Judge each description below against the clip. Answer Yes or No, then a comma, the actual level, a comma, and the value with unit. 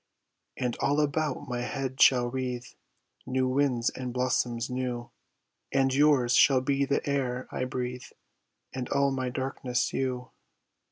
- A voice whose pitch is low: Yes, low, 130 Hz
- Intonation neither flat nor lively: No, narrow, 1.6 semitones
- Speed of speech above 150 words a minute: No, slow, 135 wpm